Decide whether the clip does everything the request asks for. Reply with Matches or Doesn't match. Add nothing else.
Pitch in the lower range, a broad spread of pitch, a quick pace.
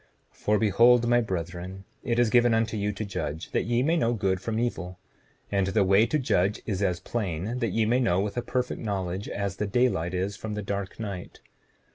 Doesn't match